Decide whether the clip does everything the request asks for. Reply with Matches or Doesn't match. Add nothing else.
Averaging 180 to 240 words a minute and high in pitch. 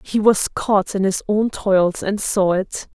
Matches